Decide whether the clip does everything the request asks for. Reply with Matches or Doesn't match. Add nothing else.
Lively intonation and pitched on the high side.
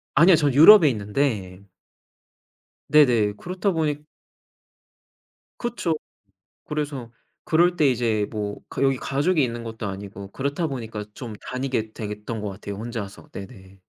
Doesn't match